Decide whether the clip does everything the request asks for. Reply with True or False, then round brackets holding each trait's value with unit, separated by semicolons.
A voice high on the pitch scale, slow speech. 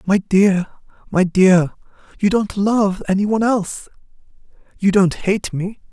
True (195 Hz; 130 wpm)